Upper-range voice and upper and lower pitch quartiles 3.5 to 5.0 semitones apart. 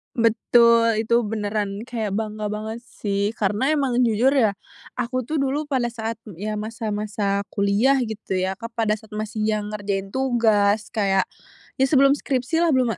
No: high, 220 Hz; average, 2.9 semitones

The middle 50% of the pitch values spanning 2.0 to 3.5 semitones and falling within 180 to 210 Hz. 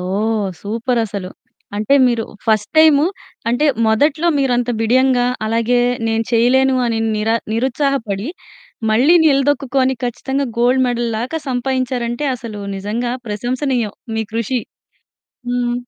No: average, 2.9 semitones; high, 240 Hz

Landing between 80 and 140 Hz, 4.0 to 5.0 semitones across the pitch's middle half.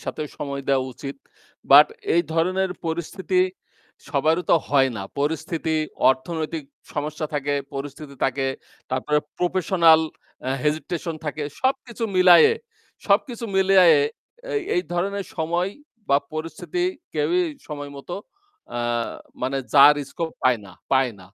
No: medium, 160 Hz; average, 4.3 semitones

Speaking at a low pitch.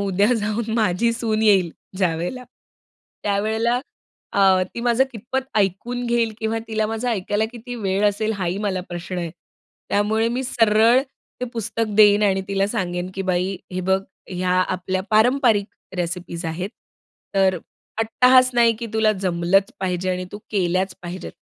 No: high, 205 Hz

